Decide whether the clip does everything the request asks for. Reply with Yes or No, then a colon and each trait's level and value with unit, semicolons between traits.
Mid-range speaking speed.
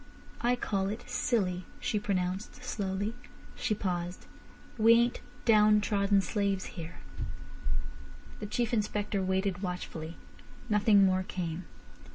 No: slow, 110 wpm